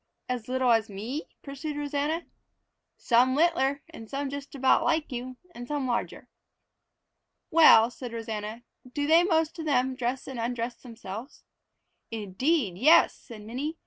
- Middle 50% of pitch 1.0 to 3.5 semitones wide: No, average, 4.0 semitones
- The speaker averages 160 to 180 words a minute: No, average, 145 wpm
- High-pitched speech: Yes, very high, 255 Hz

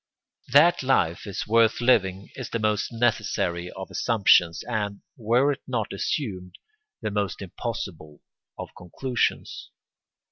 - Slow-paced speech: Yes, slow, 120 wpm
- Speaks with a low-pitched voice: Yes, low, 105 Hz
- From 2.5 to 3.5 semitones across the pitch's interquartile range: No, average, 4.2 semitones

